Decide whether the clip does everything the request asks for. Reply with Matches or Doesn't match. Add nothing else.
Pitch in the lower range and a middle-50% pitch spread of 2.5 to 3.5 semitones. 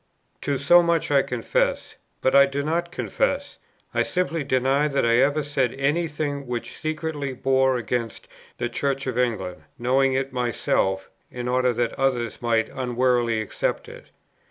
Matches